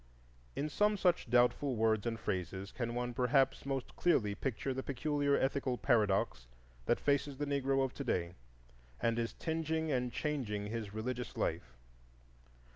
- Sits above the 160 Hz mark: No, low, 125 Hz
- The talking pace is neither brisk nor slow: Yes, average, 150 wpm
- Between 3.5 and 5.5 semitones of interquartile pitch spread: Yes, average, 4.1 semitones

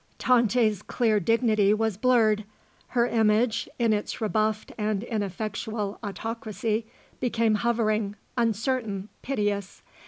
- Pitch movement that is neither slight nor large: No, narrow, 1.7 semitones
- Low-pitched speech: No, high, 220 Hz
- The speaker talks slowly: Yes, slow, 100 wpm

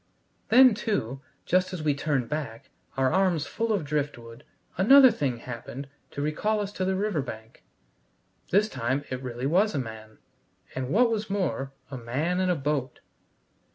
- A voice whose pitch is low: No, medium, 150 Hz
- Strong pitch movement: Yes, wide, 7.2 semitones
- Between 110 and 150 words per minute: No, average, 165 wpm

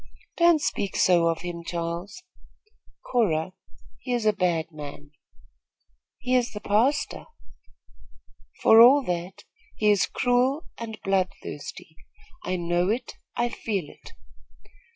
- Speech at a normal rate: No, slow, 120 wpm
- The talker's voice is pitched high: Yes, high, 200 Hz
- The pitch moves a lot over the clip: Yes, wide, 6.0 semitones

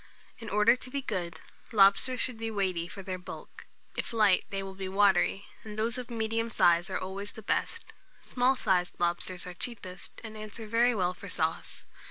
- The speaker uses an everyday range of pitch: Yes, average, 3.5 semitones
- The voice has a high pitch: Yes, high, 205 Hz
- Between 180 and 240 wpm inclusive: Yes, average, 195 wpm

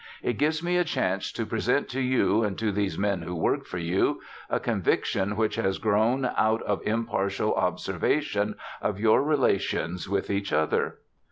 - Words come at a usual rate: Yes, average, 170 wpm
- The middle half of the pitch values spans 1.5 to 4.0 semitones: Yes, average, 3.4 semitones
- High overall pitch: No, low, 105 Hz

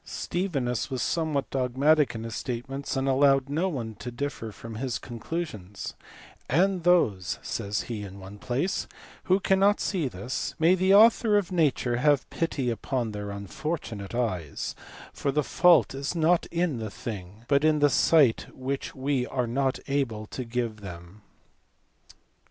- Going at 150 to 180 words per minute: Yes, average, 155 wpm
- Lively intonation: Yes, wide, 5.8 semitones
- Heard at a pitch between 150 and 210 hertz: No, low, 130 Hz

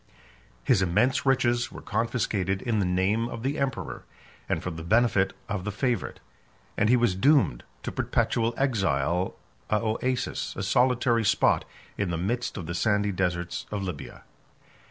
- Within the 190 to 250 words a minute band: No, average, 155 wpm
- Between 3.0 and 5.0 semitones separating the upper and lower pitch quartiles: Yes, average, 4.4 semitones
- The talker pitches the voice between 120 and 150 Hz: No, low, 105 Hz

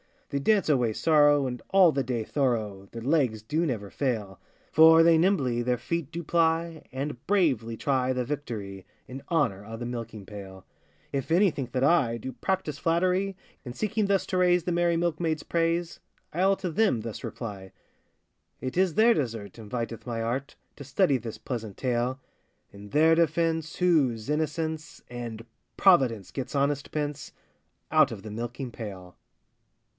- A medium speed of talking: Yes, average, 160 wpm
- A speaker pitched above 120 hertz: Yes, medium, 140 Hz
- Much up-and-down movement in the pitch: Yes, wide, 6.2 semitones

